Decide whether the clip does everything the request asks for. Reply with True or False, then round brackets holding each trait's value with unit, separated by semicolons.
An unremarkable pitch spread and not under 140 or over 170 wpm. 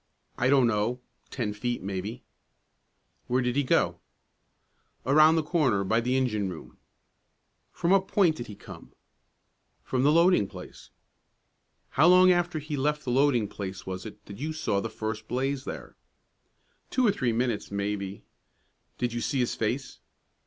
False (6.1 semitones; 160 wpm)